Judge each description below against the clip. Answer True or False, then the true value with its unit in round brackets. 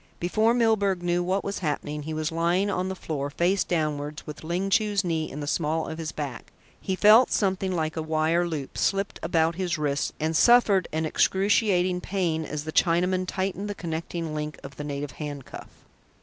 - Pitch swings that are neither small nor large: True (3.5 semitones)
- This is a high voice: False (170 Hz)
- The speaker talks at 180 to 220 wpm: True (190 wpm)